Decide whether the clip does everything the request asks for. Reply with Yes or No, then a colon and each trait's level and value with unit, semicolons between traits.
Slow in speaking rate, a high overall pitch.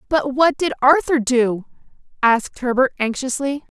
Yes: slow, 125 wpm; very high, 260 Hz